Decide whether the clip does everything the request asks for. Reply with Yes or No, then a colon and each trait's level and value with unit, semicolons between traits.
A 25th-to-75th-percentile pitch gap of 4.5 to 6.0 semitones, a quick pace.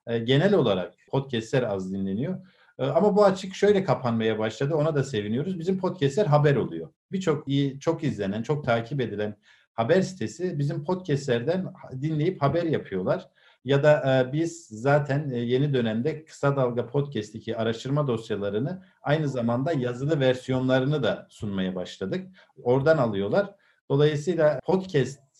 No: average, 5.3 semitones; average, 130 wpm